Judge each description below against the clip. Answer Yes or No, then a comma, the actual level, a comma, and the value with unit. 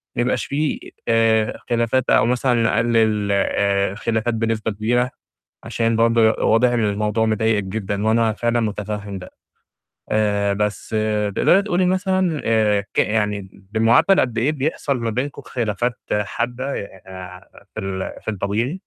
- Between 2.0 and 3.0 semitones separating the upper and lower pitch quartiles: Yes, average, 2.7 semitones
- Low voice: Yes, low, 110 Hz